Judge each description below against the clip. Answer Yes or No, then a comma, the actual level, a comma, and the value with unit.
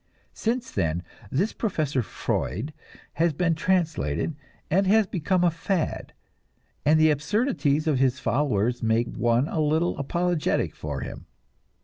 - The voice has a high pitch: No, medium, 155 Hz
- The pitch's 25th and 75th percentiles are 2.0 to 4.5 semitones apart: No, average, 5.3 semitones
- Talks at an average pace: No, slow, 130 wpm